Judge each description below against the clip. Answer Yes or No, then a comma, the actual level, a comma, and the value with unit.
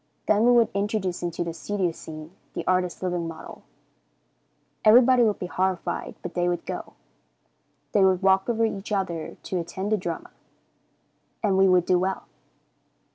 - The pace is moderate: Yes, average, 160 wpm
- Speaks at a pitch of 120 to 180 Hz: No, high, 190 Hz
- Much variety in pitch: No, average, 2.8 semitones